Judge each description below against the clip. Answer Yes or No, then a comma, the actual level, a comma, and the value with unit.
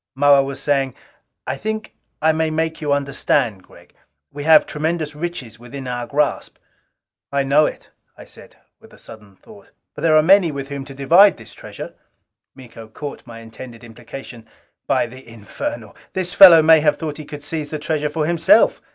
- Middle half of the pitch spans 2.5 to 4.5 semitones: Yes, average, 4.2 semitones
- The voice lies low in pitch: No, medium, 145 Hz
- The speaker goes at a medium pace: Yes, average, 175 wpm